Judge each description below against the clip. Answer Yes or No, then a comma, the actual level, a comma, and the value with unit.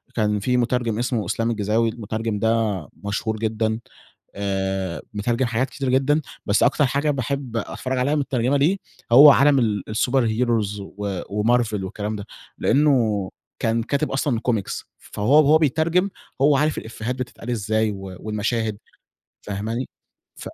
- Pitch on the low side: Yes, low, 115 Hz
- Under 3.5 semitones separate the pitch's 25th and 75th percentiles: No, average, 4.0 semitones